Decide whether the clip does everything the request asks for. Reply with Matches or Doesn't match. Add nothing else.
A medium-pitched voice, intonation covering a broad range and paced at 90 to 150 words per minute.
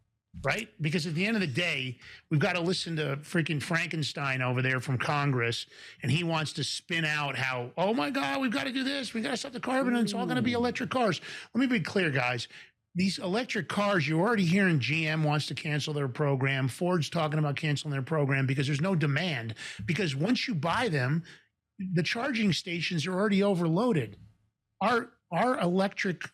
Doesn't match